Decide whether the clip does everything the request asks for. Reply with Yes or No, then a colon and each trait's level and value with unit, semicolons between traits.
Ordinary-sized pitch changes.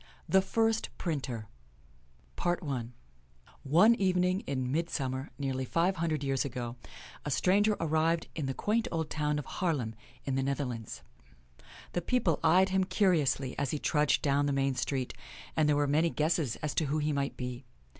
Yes: average, 4.3 semitones